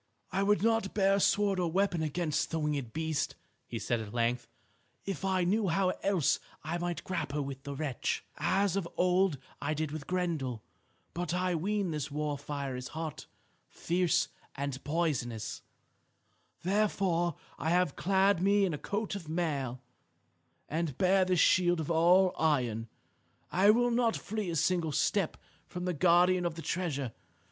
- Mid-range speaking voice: Yes, medium, 170 Hz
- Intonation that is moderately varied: Yes, average, 4.3 semitones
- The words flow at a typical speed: Yes, average, 165 wpm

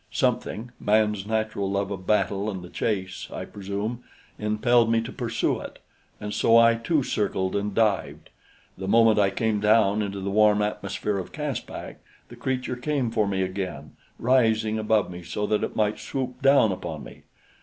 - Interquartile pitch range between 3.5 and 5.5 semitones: No, narrow, 2.6 semitones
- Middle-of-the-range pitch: No, low, 105 Hz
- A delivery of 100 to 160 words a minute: No, average, 175 wpm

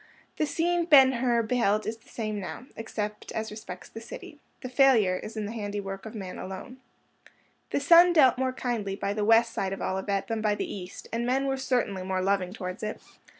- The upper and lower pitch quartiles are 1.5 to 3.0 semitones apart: No, average, 4.2 semitones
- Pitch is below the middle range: No, high, 220 Hz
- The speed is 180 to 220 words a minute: Yes, fast, 205 wpm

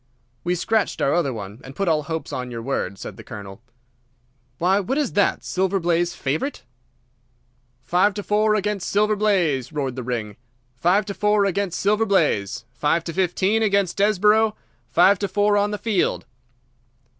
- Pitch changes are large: Yes, wide, 6.5 semitones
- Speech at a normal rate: Yes, average, 170 wpm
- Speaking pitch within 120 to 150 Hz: No, medium, 185 Hz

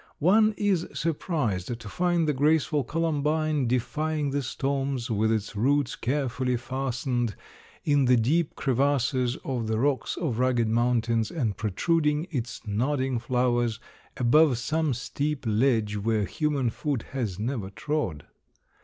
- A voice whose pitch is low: Yes, low, 130 Hz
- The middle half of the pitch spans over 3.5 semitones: Yes, average, 4.3 semitones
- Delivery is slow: Yes, slow, 130 wpm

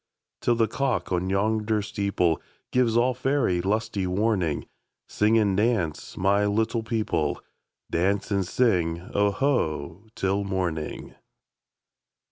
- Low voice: Yes, low, 100 Hz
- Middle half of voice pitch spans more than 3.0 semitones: Yes, average, 3.7 semitones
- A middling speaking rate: No, slow, 95 wpm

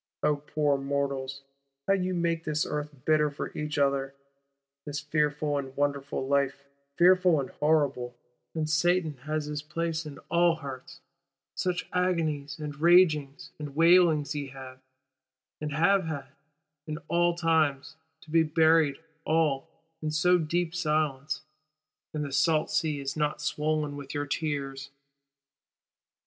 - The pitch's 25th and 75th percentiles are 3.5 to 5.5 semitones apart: No, narrow, 2.4 semitones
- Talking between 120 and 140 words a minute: Yes, slow, 135 wpm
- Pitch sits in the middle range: Yes, medium, 150 Hz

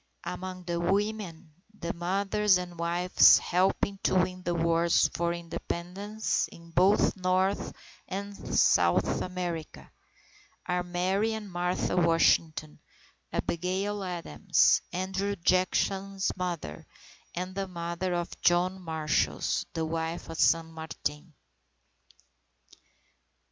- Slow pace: Yes, slow, 105 wpm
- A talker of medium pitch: Yes, medium, 180 Hz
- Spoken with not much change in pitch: Yes, narrow, 2.1 semitones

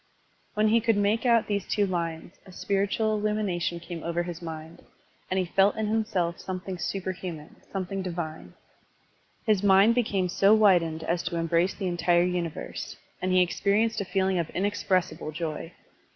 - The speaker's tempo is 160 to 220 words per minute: Yes, average, 165 wpm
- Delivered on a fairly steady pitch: No, average, 3.0 semitones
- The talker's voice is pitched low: No, medium, 185 Hz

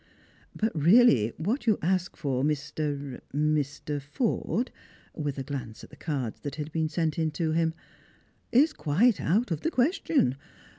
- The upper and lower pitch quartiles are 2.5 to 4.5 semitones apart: No, wide, 5.4 semitones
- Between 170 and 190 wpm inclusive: No, average, 160 wpm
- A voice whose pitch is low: No, medium, 155 Hz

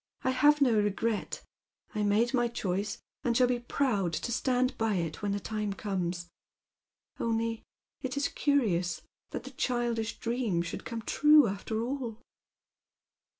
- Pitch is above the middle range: Yes, high, 230 Hz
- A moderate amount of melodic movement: Yes, average, 3.7 semitones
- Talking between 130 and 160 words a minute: Yes, average, 150 wpm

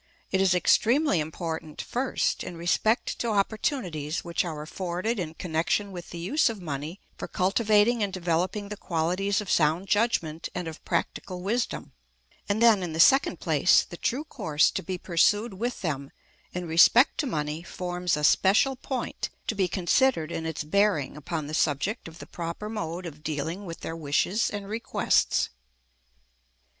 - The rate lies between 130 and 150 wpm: No, average, 165 wpm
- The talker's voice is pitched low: No, medium, 180 Hz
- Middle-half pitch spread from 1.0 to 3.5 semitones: No, average, 4.5 semitones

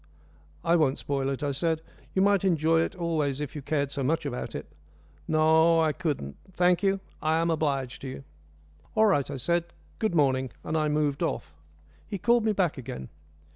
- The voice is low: No, medium, 155 Hz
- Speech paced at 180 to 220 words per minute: Yes, average, 190 wpm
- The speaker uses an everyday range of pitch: Yes, average, 3.5 semitones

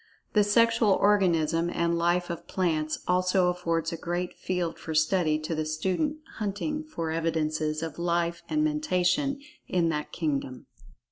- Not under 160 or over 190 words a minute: No, average, 145 wpm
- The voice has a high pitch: No, medium, 175 Hz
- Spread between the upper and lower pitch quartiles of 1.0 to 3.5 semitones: Yes, average, 3.2 semitones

